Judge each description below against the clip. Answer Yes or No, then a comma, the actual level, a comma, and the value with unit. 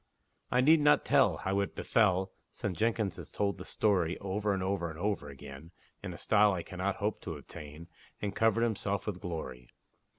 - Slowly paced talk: No, average, 190 wpm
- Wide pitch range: No, average, 3.4 semitones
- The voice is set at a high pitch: No, low, 100 Hz